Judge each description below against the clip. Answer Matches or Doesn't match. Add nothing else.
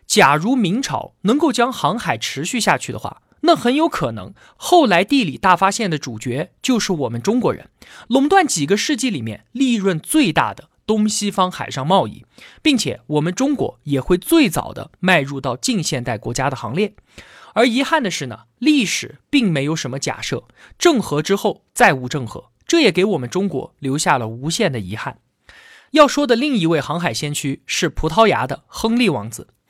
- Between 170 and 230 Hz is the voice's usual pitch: Matches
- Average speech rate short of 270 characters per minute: Doesn't match